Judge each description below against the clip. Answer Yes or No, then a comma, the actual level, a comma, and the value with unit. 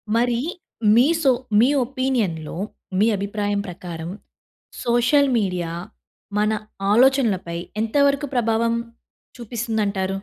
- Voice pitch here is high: Yes, high, 220 Hz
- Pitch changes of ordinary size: Yes, average, 4.1 semitones